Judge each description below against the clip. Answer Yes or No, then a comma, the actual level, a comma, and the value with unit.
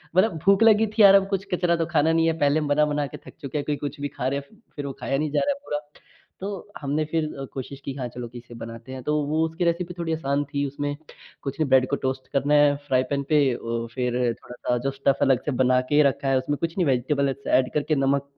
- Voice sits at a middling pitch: Yes, medium, 145 Hz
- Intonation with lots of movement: No, average, 3.3 semitones